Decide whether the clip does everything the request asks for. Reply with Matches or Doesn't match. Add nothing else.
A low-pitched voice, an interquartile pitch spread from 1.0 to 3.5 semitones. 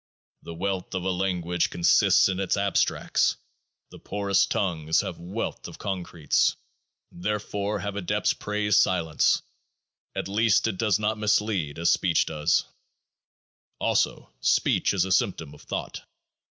Matches